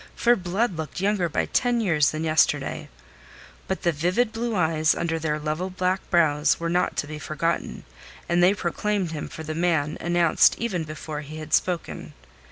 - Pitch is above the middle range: No, medium, 170 Hz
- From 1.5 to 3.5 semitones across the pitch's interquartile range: Yes, average, 3.1 semitones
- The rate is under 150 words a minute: No, average, 175 wpm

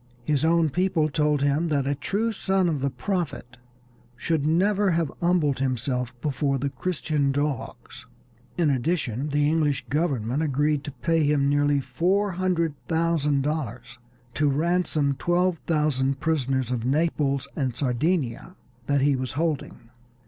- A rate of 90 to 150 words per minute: Yes, average, 140 wpm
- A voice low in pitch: No, medium, 150 Hz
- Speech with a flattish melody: No, average, 3.5 semitones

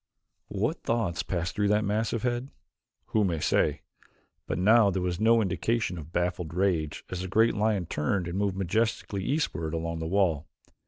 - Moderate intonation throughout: Yes, average, 4.2 semitones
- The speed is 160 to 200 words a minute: Yes, average, 170 wpm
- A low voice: Yes, very low, 95 Hz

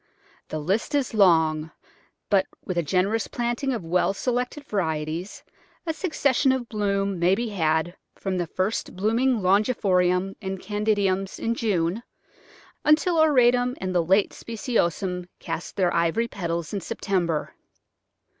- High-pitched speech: Yes, high, 195 Hz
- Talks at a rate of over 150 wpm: No, slow, 135 wpm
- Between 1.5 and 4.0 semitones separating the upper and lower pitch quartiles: No, average, 4.9 semitones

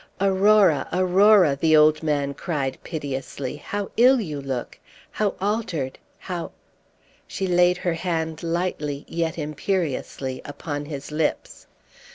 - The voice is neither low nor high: Yes, medium, 160 Hz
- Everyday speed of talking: No, slow, 125 wpm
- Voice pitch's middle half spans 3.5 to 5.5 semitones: Yes, average, 4.3 semitones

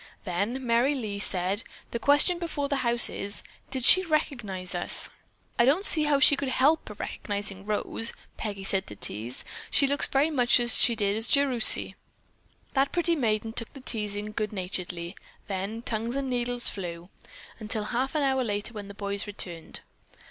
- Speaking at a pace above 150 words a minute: Yes, average, 170 wpm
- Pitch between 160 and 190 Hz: No, high, 230 Hz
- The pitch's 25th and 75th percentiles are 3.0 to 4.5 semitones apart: No, average, 5.1 semitones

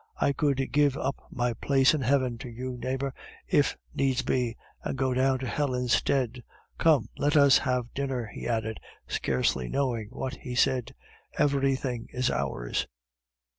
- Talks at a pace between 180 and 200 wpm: No, average, 155 wpm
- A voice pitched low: Yes, low, 130 Hz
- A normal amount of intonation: No, narrow, 2.2 semitones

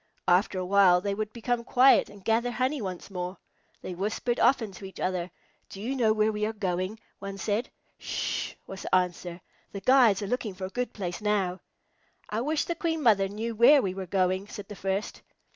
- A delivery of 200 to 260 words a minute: Yes, fast, 205 wpm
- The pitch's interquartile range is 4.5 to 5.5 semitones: No, average, 3.8 semitones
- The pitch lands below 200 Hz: No, high, 205 Hz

